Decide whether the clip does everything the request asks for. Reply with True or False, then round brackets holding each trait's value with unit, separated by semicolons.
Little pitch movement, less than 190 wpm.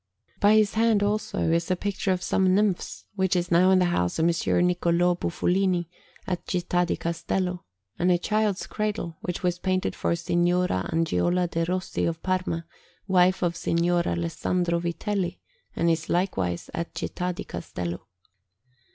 True (1.7 semitones; 160 wpm)